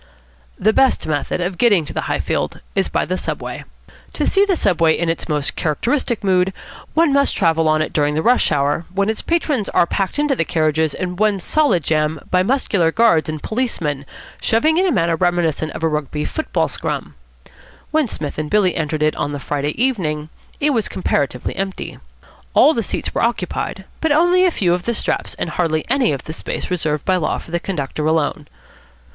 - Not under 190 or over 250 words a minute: Yes, average, 200 wpm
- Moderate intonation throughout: No, wide, 7.0 semitones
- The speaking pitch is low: No, medium, 175 Hz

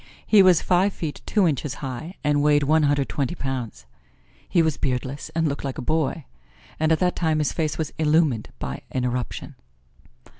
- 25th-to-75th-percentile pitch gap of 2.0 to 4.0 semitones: Yes, average, 3.3 semitones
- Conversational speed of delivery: Yes, average, 185 wpm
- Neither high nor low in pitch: Yes, medium, 150 Hz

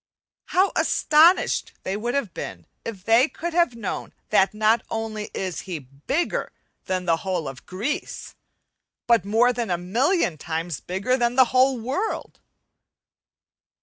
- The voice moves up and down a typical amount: No, wide, 6.0 semitones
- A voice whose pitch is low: No, high, 225 Hz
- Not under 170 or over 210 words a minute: No, average, 145 wpm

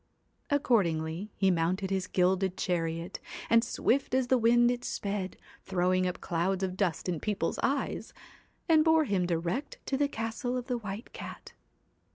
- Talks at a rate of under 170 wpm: Yes, average, 160 wpm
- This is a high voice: Yes, high, 195 Hz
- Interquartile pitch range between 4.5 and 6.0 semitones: Yes, average, 5.0 semitones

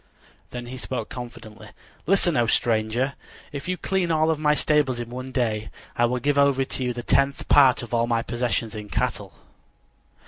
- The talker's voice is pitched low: Yes, low, 125 Hz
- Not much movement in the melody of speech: No, average, 3.1 semitones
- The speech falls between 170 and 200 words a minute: Yes, average, 185 wpm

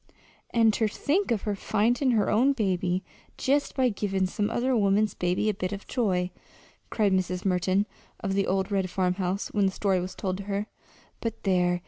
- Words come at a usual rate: Yes, average, 185 wpm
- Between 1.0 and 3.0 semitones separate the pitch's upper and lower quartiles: Yes, average, 2.7 semitones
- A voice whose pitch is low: No, high, 200 Hz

